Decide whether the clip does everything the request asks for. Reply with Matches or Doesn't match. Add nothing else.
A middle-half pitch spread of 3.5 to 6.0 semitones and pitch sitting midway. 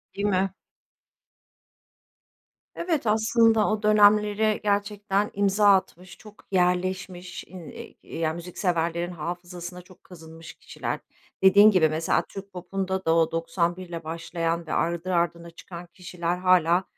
Doesn't match